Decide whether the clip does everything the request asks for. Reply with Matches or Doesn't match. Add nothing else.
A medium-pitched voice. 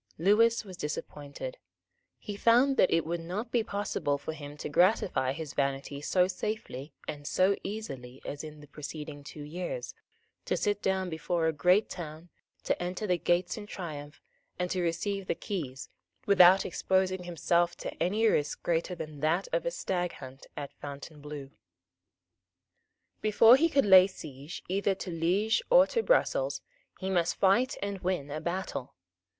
Matches